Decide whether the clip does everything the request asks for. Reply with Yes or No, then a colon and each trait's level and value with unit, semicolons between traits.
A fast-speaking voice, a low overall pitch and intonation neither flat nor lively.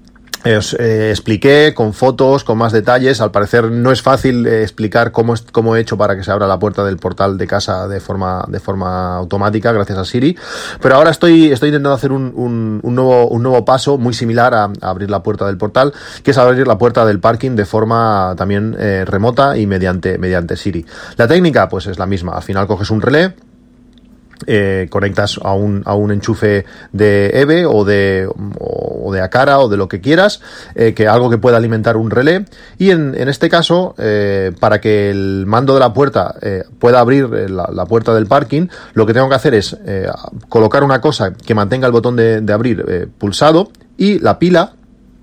Yes: fast, 210 wpm; low, 115 Hz; average, 4.7 semitones